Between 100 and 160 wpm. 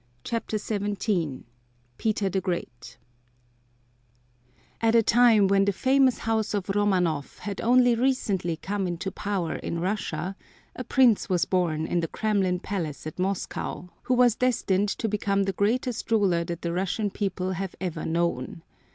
Yes: average, 150 wpm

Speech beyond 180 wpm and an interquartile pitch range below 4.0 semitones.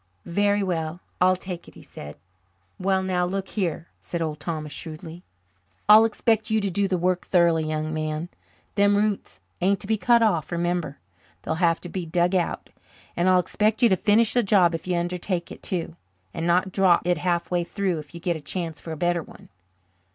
Yes: average, 200 wpm; average, 2.8 semitones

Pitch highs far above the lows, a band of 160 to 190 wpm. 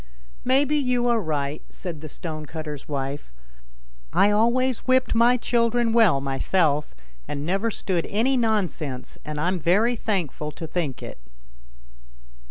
No: wide, 7.7 semitones; slow, 135 wpm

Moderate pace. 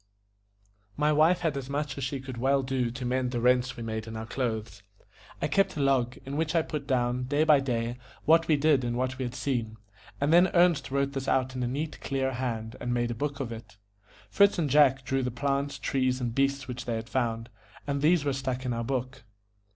No: fast, 230 wpm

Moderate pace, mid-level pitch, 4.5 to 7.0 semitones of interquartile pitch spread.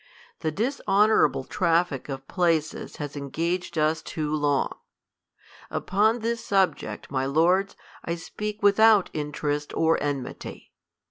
No: slow, 115 wpm; medium, 165 Hz; average, 5.1 semitones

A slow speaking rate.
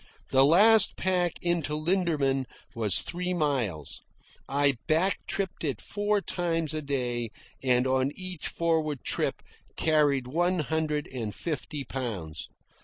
Yes: slow, 125 wpm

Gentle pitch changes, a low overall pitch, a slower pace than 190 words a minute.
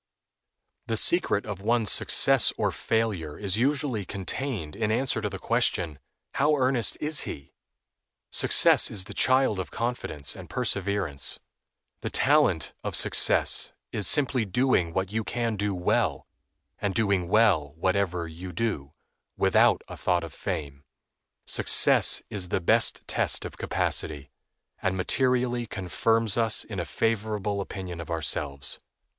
No: average, 4.6 semitones; low, 100 Hz; average, 140 wpm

